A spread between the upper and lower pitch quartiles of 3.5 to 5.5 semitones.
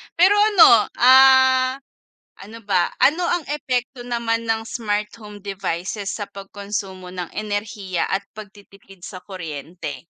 Yes: average, 4.3 semitones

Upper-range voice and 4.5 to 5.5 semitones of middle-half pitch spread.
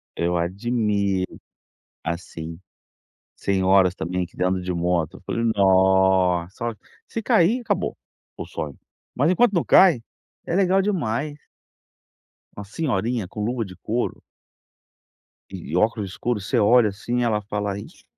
No: low, 100 Hz; average, 4.9 semitones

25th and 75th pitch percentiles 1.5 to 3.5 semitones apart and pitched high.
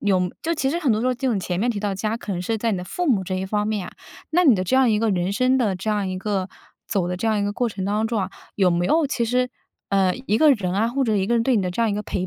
No: average, 4.1 semitones; high, 210 Hz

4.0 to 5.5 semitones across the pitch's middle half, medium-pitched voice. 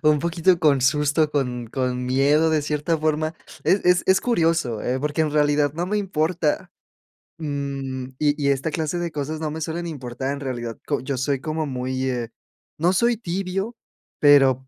No: average, 3.5 semitones; medium, 150 Hz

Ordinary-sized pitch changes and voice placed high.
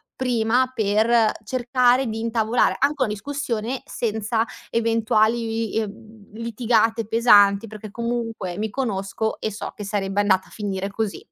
No: narrow, 2.1 semitones; high, 225 Hz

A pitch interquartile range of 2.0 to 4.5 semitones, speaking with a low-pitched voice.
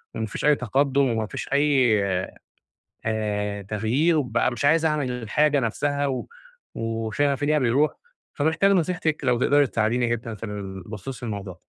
No: average, 4.9 semitones; low, 125 Hz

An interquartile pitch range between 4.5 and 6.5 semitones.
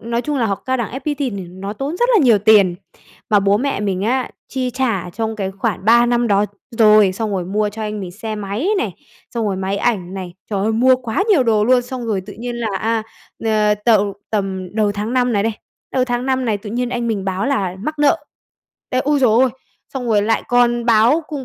No: average, 3.6 semitones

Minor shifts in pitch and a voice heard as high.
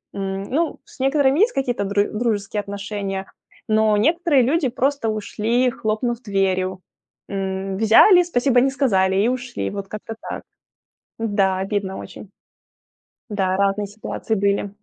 No: average, 4.3 semitones; high, 215 Hz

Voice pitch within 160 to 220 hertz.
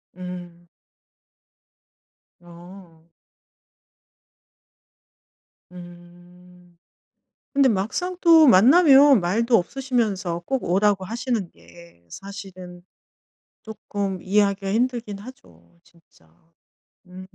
Yes: high, 190 Hz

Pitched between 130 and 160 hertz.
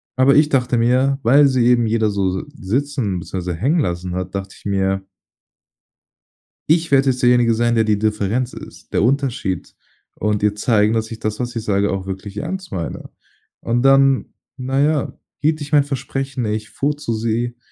No: low, 120 Hz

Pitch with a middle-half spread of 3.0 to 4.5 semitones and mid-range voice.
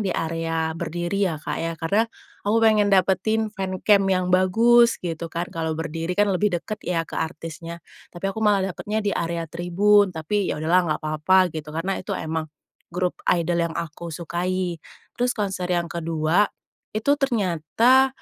Yes: average, 3.6 semitones; medium, 180 Hz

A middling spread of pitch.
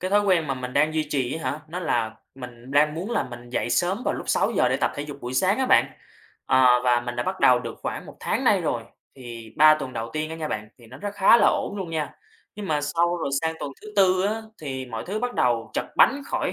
No: wide, 6.6 semitones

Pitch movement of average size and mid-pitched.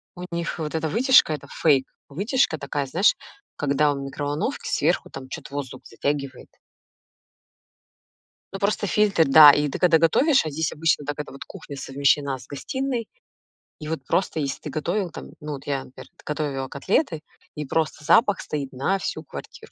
Yes: average, 4.0 semitones; medium, 150 Hz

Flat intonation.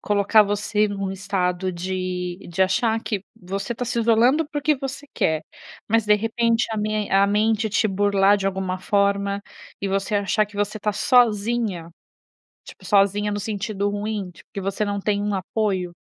Yes: narrow, 2.0 semitones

